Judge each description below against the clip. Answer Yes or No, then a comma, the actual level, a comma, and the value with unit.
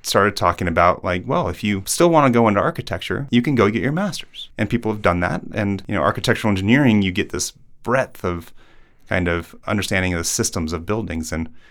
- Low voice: Yes, low, 100 Hz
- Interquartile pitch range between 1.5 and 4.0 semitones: No, average, 4.7 semitones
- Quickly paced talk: Yes, fast, 220 wpm